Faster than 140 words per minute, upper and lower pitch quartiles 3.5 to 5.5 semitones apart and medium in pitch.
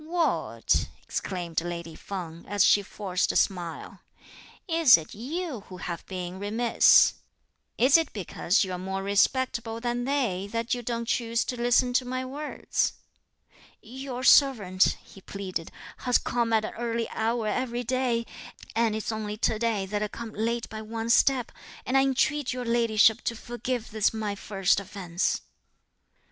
No: average, 155 wpm; average, 3.8 semitones; high, 225 Hz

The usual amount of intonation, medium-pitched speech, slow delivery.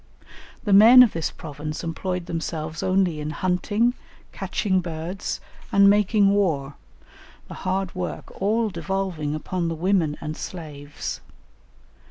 Yes: average, 4.0 semitones; medium, 180 Hz; slow, 125 wpm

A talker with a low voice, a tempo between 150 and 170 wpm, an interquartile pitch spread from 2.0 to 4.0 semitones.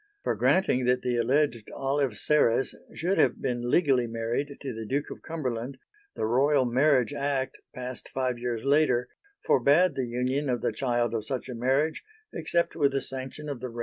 No: low, 130 Hz; average, 185 wpm; average, 2.9 semitones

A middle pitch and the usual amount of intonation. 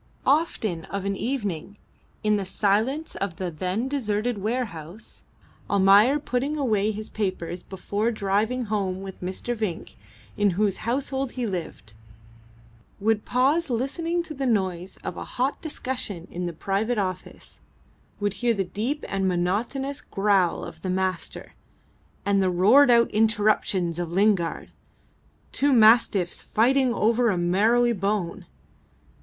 No: high, 210 Hz; average, 4.4 semitones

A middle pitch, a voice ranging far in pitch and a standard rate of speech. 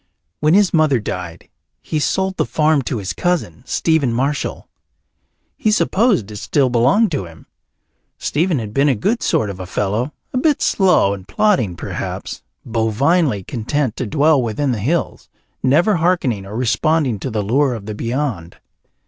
No: low, 130 Hz; wide, 6.9 semitones; average, 165 wpm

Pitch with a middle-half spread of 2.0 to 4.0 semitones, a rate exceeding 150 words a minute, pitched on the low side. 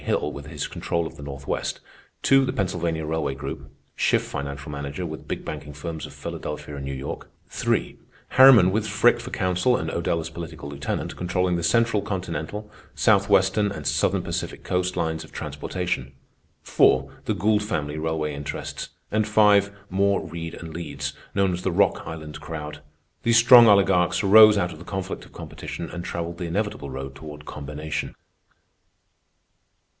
No: average, 5.0 semitones; average, 165 wpm; very low, 85 Hz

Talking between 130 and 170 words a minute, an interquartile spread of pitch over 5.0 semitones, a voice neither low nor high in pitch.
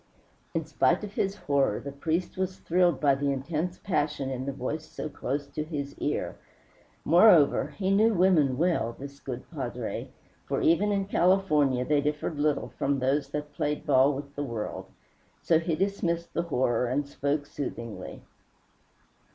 No: average, 160 wpm; average, 3.7 semitones; medium, 150 Hz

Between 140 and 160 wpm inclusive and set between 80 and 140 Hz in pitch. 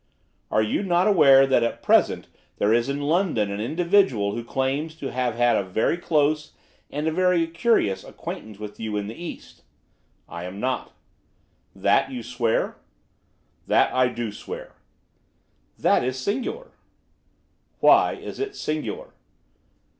Yes: average, 145 wpm; low, 135 Hz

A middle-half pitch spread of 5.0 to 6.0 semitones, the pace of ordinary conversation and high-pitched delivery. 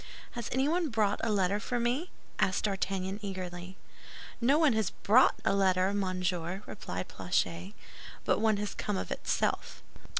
No: average, 3.4 semitones; average, 145 wpm; high, 200 Hz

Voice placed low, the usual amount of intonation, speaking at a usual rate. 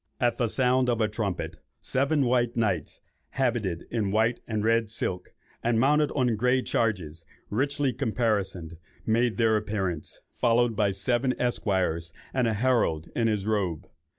Yes: low, 115 Hz; average, 3.6 semitones; average, 150 wpm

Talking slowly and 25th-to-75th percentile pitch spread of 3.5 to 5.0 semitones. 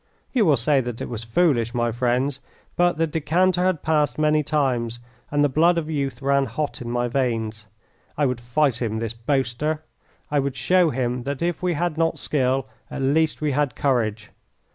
No: average, 190 wpm; average, 4.2 semitones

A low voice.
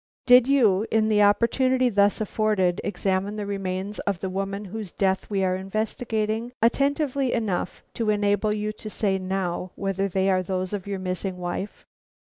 No: high, 205 Hz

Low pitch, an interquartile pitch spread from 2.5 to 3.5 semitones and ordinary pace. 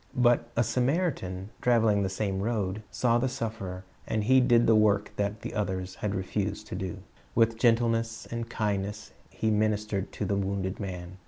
Yes: low, 105 Hz; average, 2.9 semitones; average, 175 wpm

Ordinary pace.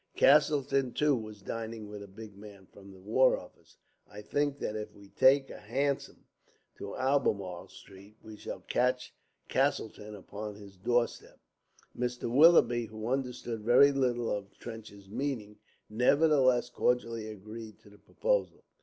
Yes: average, 150 wpm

